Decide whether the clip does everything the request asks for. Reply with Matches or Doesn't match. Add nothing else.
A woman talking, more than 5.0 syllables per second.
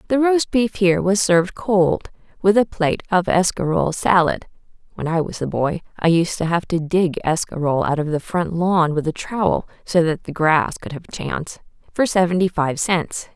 Doesn't match